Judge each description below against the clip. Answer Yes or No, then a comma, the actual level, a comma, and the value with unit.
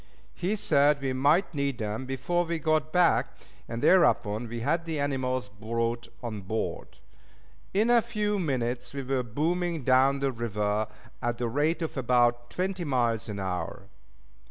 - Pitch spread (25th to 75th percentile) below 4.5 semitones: No, wide, 5.6 semitones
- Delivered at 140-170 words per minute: Yes, average, 155 wpm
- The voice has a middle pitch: No, low, 130 Hz